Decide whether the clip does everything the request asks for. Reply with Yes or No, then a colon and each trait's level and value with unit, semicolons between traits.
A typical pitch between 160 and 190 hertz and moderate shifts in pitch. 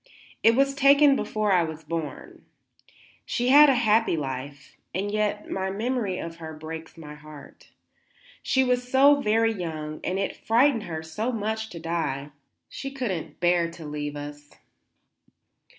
No: medium, 185 Hz; wide, 6.9 semitones